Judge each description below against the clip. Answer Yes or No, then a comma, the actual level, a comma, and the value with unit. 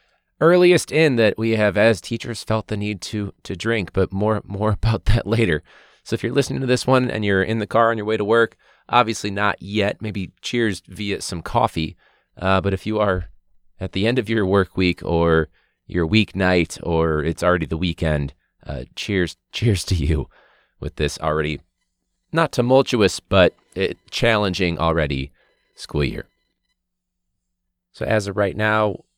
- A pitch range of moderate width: Yes, average, 4.1 semitones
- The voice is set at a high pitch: No, low, 100 Hz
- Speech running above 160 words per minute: Yes, average, 175 wpm